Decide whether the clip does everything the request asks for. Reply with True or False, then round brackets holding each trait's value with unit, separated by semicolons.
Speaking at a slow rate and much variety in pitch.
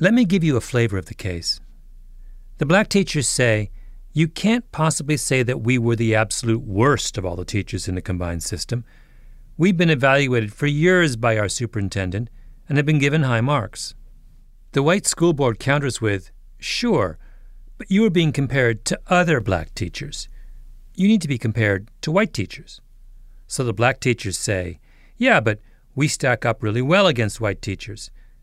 False (175 wpm; 5.9 semitones)